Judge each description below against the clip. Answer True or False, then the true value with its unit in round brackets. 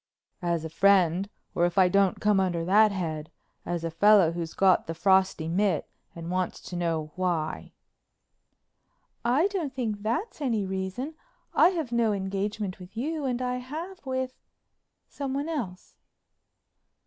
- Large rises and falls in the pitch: True (6.1 semitones)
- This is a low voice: False (195 Hz)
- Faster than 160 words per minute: False (145 wpm)